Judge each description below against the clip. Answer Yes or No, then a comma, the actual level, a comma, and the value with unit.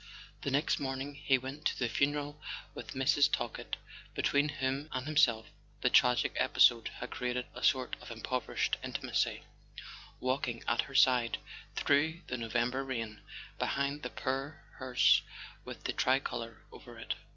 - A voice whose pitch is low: Yes, low, 130 Hz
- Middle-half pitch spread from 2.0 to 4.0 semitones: Yes, narrow, 2.4 semitones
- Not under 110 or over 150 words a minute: Yes, average, 140 wpm